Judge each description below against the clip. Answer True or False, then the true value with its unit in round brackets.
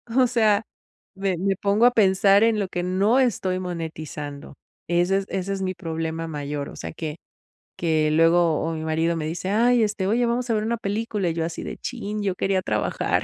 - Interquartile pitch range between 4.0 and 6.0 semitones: True (4.4 semitones)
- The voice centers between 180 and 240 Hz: True (190 Hz)